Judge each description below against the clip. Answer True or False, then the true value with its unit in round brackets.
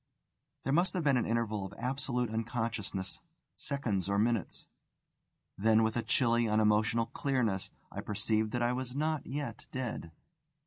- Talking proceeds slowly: False (145 wpm)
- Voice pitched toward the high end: False (115 Hz)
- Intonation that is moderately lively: True (3.2 semitones)